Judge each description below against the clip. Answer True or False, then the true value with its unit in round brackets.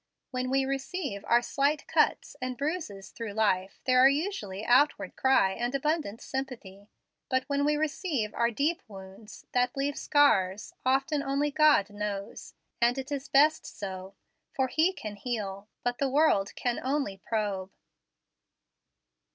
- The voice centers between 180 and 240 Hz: False (255 Hz)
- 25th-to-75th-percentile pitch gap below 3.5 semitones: False (5.6 semitones)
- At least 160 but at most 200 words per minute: False (145 wpm)